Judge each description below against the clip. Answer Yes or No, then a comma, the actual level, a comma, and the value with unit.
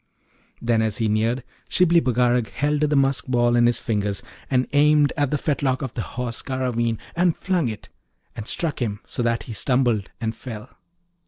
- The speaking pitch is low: Yes, low, 125 Hz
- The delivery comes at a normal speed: Yes, average, 180 wpm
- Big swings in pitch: No, average, 3.8 semitones